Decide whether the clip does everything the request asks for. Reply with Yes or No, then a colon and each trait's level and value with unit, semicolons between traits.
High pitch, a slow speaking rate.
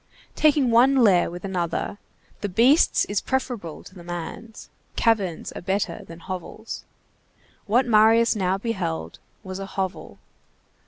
Yes: high, 200 Hz; slow, 130 wpm